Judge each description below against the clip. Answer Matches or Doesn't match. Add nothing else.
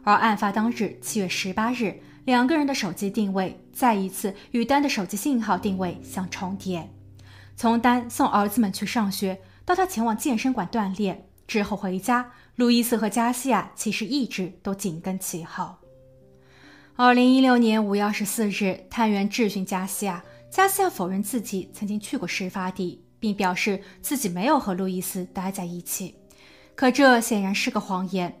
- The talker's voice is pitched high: Matches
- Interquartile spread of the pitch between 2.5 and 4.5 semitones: Matches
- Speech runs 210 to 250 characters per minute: Doesn't match